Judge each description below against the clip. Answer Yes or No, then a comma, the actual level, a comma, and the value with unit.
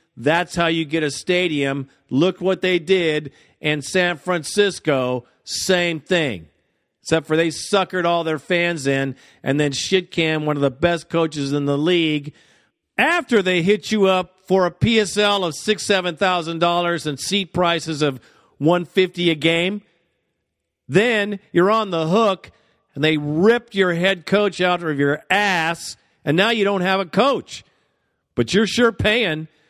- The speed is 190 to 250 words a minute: No, average, 165 wpm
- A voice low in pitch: No, medium, 175 Hz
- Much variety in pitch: No, average, 3.6 semitones